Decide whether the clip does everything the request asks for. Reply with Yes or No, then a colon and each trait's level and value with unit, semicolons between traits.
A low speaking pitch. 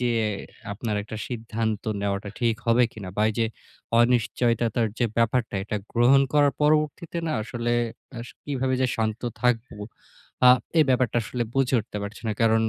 Yes: low, 120 Hz